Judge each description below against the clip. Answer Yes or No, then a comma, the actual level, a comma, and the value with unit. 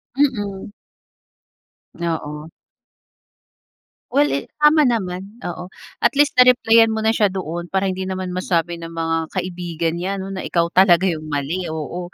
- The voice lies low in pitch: No, medium, 185 Hz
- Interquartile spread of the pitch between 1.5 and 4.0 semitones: Yes, average, 3.1 semitones